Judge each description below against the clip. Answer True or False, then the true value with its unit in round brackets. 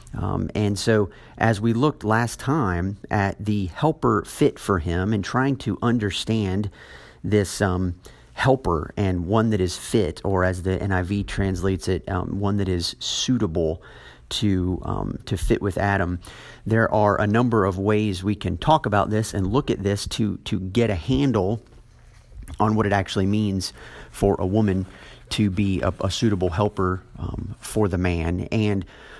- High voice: False (100 Hz)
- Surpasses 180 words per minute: False (170 wpm)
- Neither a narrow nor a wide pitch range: True (3.0 semitones)